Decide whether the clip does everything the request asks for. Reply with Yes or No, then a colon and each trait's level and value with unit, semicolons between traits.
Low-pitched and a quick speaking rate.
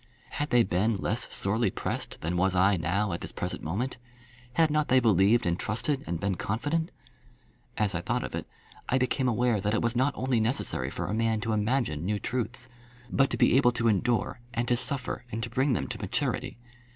Yes: low, 115 Hz; fast, 210 wpm